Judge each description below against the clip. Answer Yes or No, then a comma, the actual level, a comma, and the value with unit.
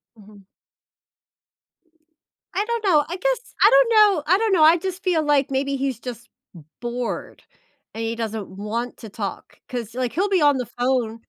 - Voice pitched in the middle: No, very high, 270 Hz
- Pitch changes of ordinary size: No, wide, 8.2 semitones